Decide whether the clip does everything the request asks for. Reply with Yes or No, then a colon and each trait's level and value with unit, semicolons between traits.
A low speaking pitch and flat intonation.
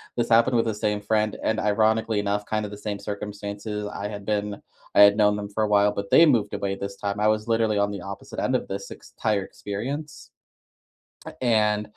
Yes: low, 105 Hz; narrow, 1.3 semitones